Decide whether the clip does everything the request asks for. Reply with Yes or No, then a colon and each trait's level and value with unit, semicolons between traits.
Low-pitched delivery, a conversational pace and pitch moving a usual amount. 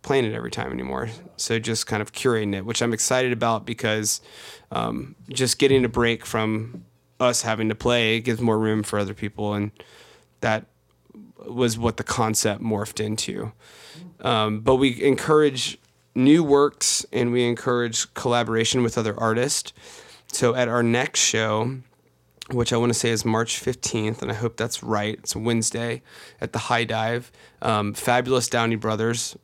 No: low, 115 Hz; average, 165 wpm; narrow, 2.1 semitones